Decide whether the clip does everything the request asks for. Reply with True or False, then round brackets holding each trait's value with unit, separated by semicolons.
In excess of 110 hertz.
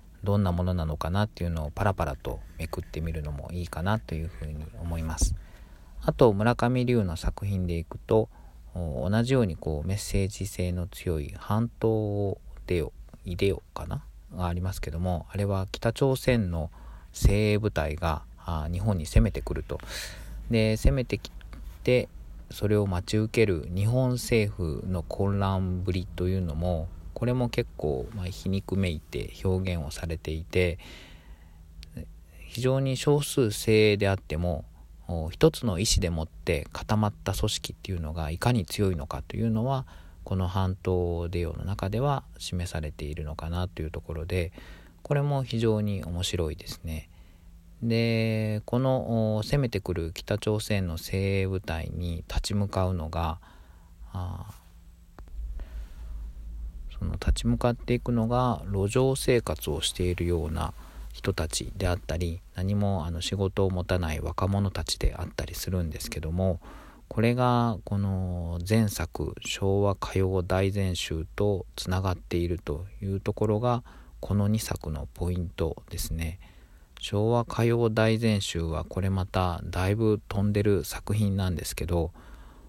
False (90 Hz)